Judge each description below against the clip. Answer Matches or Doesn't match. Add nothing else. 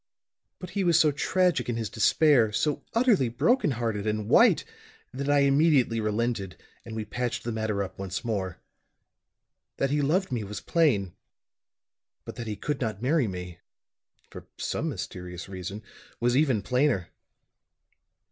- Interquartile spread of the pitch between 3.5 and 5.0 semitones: Doesn't match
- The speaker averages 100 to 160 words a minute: Matches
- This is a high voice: Doesn't match